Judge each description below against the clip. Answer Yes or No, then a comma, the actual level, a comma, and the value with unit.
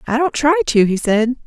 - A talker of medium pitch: No, high, 240 Hz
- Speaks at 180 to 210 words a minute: No, fast, 245 wpm